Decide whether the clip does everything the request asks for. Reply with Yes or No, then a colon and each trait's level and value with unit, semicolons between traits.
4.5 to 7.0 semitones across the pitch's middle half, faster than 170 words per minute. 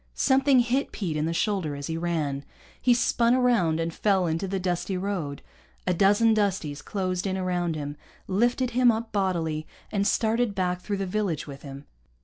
Yes: average, 5.1 semitones; average, 180 wpm